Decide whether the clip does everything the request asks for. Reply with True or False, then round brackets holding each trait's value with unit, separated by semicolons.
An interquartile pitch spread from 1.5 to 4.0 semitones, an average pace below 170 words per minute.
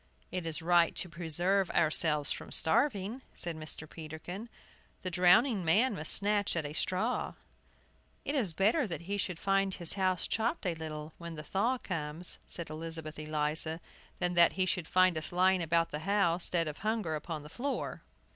False (3.5 semitones; 175 wpm)